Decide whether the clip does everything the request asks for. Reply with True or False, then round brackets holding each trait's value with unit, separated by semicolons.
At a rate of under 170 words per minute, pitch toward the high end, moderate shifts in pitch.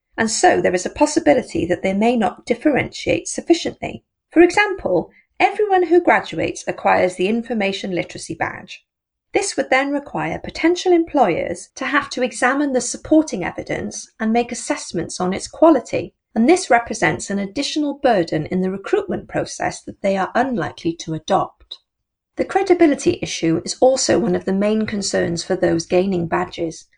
False (160 wpm; 245 Hz; 8.5 semitones)